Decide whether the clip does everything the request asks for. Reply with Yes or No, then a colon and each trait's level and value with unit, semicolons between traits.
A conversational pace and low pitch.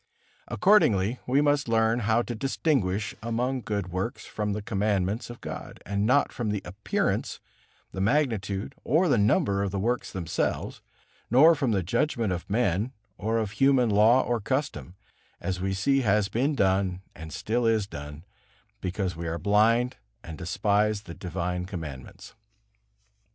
Yes: average, 155 wpm; low, 105 Hz